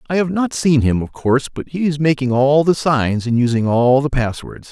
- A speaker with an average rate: No, fast, 240 wpm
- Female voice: No, male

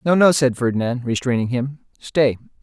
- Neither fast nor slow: Yes, average, 160 wpm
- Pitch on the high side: No, low, 130 Hz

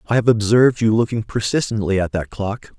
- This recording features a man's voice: Yes, male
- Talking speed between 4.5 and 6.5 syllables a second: Yes, 5.7 syllables/s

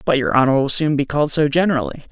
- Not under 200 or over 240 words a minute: No, fast, 255 wpm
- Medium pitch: Yes, medium, 145 Hz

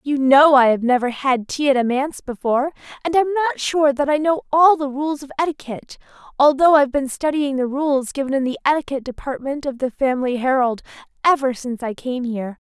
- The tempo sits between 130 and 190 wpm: No, average, 200 wpm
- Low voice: No, very high, 275 Hz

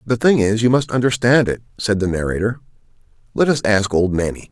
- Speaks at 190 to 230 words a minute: Yes, average, 200 wpm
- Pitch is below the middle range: Yes, low, 110 Hz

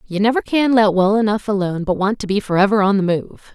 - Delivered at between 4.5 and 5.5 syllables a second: No, 6.1 syllables/s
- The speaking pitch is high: Yes, high, 205 Hz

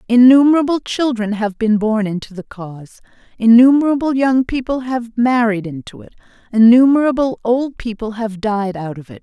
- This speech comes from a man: No, female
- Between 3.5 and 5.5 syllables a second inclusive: Yes, 5.1 syllables/s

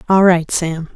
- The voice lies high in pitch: No, medium, 175 Hz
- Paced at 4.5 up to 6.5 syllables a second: No, 4.2 syllables/s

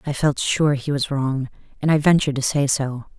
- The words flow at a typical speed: No, fast, 225 wpm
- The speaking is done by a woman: Yes, female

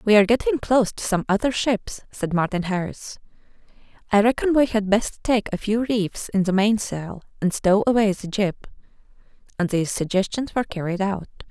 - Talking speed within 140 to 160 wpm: No, average, 175 wpm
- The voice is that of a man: No, female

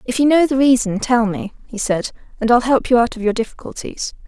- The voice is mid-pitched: No, high, 240 Hz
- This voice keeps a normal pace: No, fast, 240 wpm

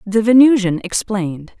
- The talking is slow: Yes, slow, 115 wpm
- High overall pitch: Yes, high, 205 Hz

